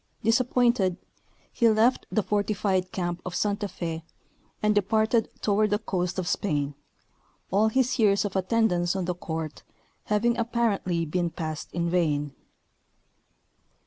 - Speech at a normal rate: No, slow, 130 wpm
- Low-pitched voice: No, high, 195 Hz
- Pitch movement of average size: Yes, average, 3.8 semitones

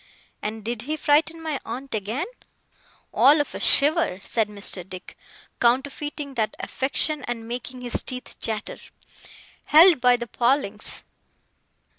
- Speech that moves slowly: Yes, slow, 130 wpm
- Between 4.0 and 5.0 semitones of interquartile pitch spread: Yes, average, 4.6 semitones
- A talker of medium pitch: No, very high, 250 Hz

